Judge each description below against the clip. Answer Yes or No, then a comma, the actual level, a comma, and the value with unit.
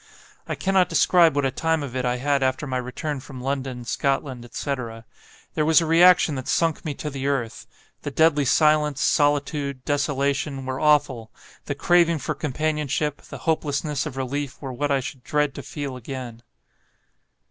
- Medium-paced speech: Yes, average, 170 wpm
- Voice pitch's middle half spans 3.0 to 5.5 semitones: No, narrow, 2.6 semitones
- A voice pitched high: No, medium, 140 Hz